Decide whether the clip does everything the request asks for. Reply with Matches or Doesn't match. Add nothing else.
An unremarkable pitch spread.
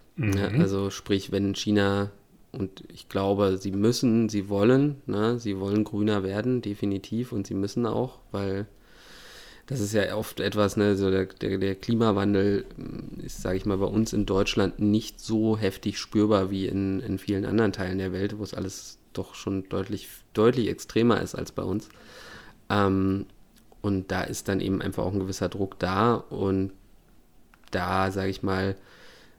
Doesn't match